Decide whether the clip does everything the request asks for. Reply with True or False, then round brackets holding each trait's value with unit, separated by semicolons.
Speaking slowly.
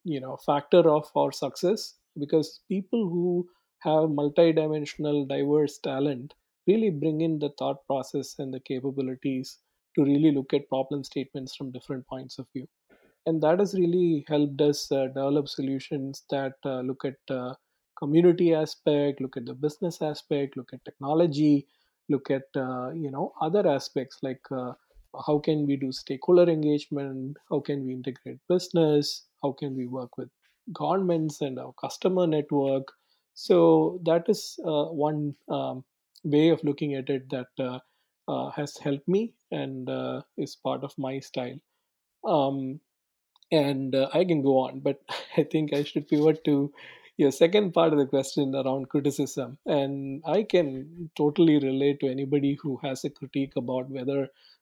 False (160 wpm)